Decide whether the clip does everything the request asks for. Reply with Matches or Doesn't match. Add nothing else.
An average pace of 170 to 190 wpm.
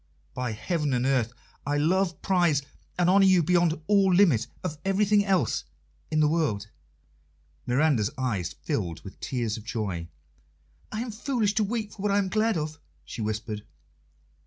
Doesn't match